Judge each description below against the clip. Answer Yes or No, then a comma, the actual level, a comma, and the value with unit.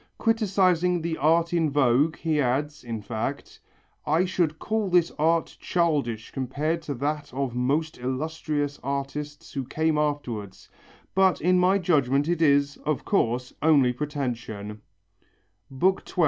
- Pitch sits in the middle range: Yes, medium, 150 Hz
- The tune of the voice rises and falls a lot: No, average, 4.1 semitones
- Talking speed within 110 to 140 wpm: Yes, slow, 135 wpm